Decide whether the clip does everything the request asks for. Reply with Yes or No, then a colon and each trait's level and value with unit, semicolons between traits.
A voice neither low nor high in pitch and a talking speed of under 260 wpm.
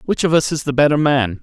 No: medium, 145 Hz; fast, 295 wpm